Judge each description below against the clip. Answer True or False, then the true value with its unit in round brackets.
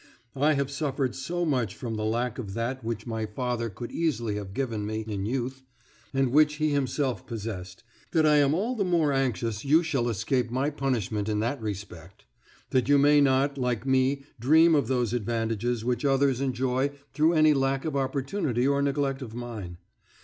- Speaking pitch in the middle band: False (130 Hz)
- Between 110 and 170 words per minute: False (185 wpm)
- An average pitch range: True (3.8 semitones)